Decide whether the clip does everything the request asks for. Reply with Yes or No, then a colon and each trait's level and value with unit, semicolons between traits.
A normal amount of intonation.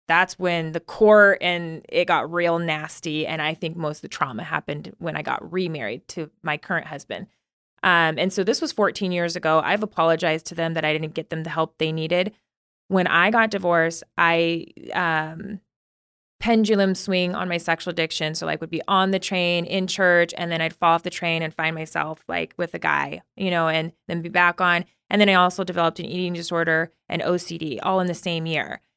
No: narrow, 2.2 semitones